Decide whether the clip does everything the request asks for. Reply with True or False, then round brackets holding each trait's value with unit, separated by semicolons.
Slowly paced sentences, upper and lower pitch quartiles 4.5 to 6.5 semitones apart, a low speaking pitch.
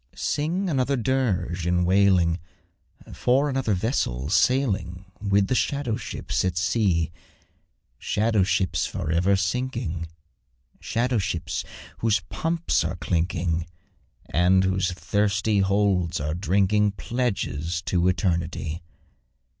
True (105 wpm; 4.8 semitones; 95 Hz)